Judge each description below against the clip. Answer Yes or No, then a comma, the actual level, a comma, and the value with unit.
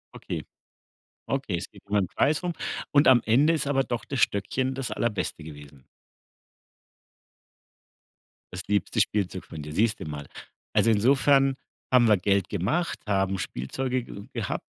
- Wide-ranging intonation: Yes, wide, 6.2 semitones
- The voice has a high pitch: No, low, 110 Hz